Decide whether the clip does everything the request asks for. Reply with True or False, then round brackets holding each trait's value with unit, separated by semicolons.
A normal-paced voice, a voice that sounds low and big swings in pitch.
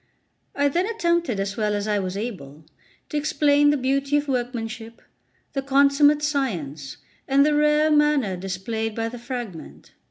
False (155 wpm; 255 Hz; 5.8 semitones)